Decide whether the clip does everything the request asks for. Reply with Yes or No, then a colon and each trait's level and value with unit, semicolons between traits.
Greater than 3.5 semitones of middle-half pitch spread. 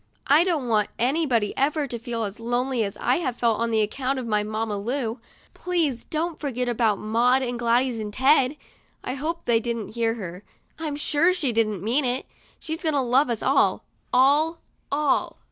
Yes: average, 4.1 semitones